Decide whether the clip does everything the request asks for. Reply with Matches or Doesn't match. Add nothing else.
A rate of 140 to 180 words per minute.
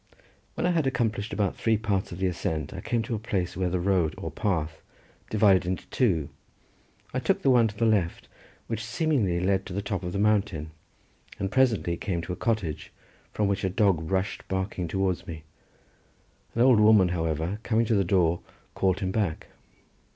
Doesn't match